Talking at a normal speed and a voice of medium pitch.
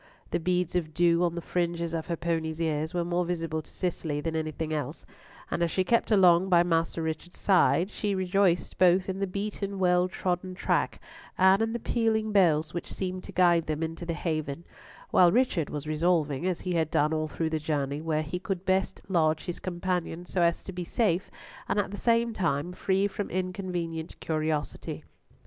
Yes: average, 195 wpm; medium, 175 Hz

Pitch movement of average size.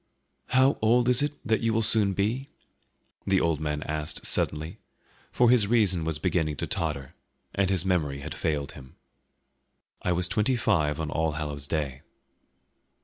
No: wide, 6.7 semitones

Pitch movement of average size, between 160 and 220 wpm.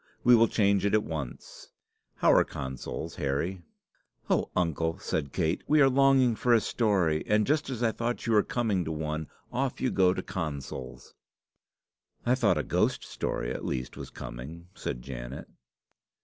No: wide, 7.4 semitones; average, 170 wpm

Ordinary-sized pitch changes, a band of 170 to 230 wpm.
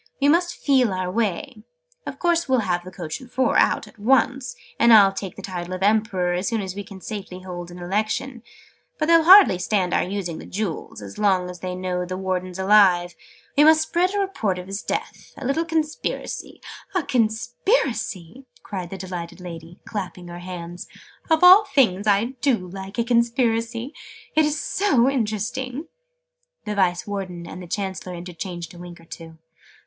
No: wide, 6.0 semitones; average, 185 wpm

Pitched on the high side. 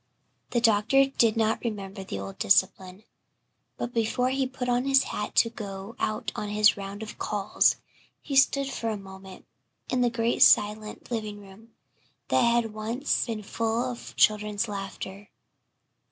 Yes: high, 220 Hz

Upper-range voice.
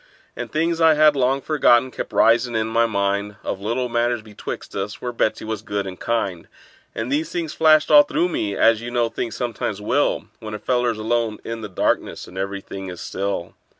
No: low, 115 Hz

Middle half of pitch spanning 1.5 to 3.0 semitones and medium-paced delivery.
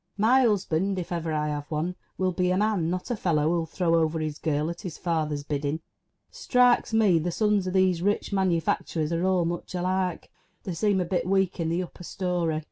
No: average, 2.7 semitones; fast, 210 wpm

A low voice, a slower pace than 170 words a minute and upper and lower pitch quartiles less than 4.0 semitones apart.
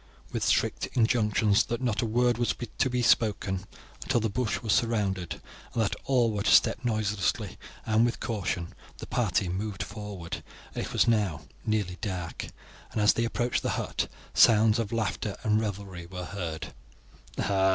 Yes: low, 105 Hz; average, 160 wpm; average, 3.1 semitones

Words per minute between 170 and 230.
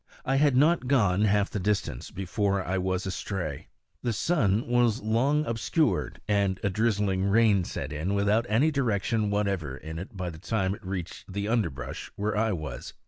Yes: average, 175 wpm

